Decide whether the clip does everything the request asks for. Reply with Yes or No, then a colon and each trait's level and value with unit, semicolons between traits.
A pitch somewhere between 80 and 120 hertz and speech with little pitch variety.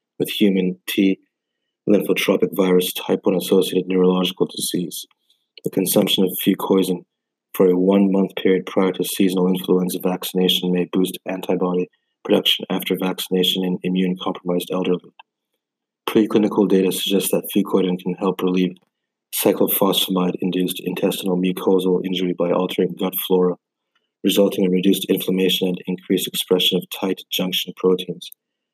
Yes: very low, 90 Hz; narrow, 0.7 semitones